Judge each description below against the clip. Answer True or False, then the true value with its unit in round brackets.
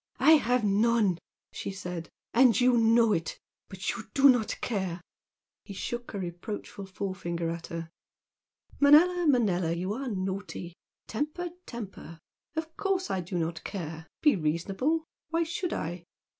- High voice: True (205 Hz)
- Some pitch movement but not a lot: False (6.3 semitones)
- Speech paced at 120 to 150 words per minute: True (145 wpm)